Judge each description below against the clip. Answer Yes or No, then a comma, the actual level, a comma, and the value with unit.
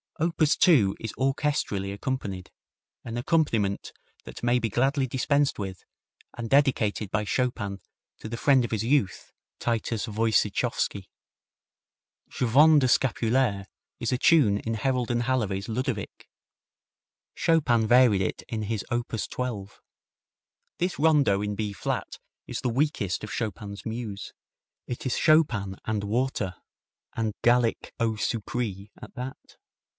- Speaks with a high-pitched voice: No, low, 115 Hz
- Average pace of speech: No, slow, 130 wpm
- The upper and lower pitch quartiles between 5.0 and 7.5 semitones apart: No, average, 4.1 semitones